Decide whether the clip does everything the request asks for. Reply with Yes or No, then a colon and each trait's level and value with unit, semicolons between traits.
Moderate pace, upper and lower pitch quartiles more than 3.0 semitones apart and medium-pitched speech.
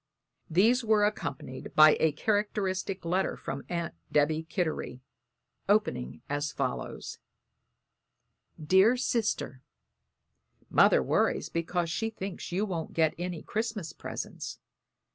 No: slow, 105 wpm; average, 5.0 semitones; medium, 175 Hz